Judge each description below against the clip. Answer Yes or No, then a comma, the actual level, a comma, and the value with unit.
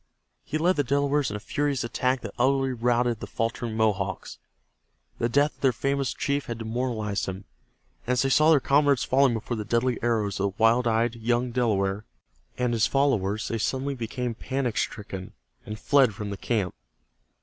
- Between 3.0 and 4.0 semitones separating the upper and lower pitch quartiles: Yes, average, 3.6 semitones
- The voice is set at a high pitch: No, low, 120 Hz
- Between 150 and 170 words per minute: No, average, 180 wpm